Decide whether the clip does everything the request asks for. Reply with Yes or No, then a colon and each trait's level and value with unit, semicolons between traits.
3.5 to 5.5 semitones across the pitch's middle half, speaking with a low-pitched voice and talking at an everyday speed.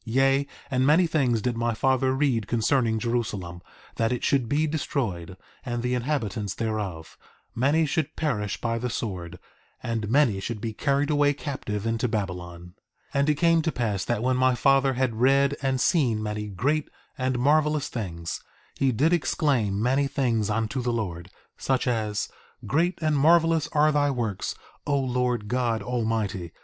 Yes: average, 4.5 semitones; low, 125 Hz; average, 160 wpm